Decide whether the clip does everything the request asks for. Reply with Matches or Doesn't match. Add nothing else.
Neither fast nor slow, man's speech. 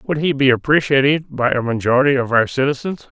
Matches